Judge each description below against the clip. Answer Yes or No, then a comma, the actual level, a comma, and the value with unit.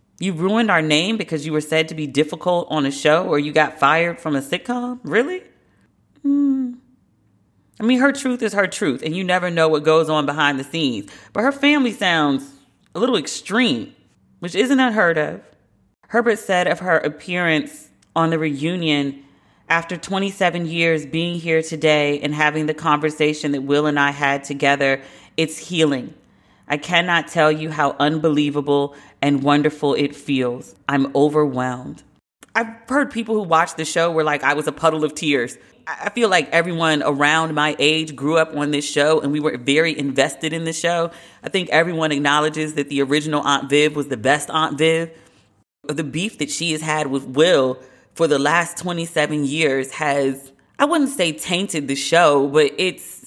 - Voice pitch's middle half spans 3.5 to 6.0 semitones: No, average, 3.0 semitones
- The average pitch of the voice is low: No, medium, 155 Hz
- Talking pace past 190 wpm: No, average, 180 wpm